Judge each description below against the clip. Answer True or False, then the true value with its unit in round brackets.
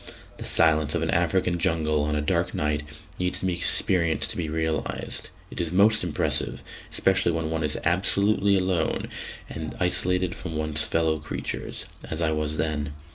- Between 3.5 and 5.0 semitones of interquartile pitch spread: False (2.8 semitones)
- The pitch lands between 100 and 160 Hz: False (80 Hz)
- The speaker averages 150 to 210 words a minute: True (170 wpm)